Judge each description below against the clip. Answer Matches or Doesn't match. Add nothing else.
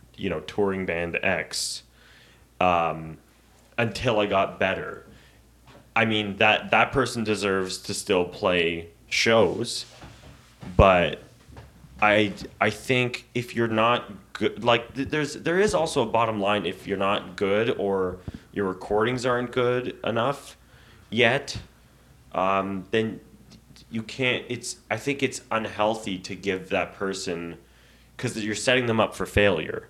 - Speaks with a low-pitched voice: Matches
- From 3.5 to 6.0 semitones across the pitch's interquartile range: Matches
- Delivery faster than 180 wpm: Doesn't match